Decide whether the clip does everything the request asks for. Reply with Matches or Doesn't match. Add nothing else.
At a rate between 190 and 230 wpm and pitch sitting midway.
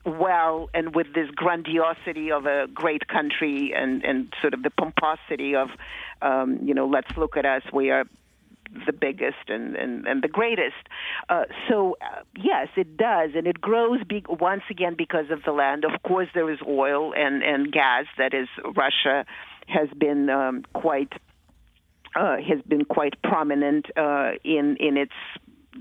Doesn't match